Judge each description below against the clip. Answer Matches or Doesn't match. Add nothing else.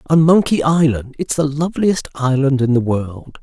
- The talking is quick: Doesn't match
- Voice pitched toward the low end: Doesn't match